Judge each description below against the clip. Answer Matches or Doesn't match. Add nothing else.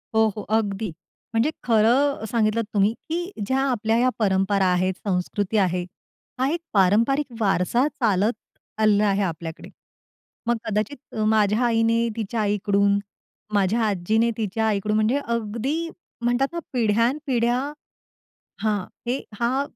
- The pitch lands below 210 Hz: Doesn't match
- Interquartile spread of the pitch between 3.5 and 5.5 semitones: Doesn't match